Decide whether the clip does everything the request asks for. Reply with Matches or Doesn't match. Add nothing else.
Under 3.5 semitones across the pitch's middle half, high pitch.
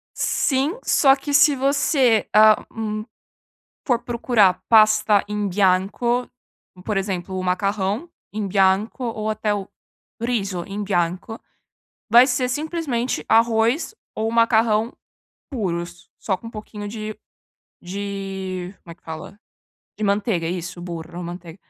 Doesn't match